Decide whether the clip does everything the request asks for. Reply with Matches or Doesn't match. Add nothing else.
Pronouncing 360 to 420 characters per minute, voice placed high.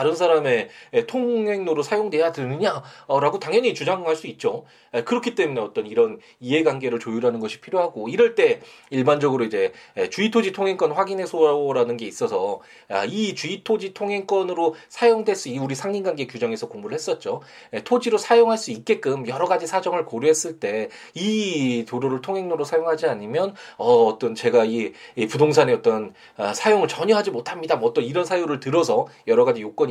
Matches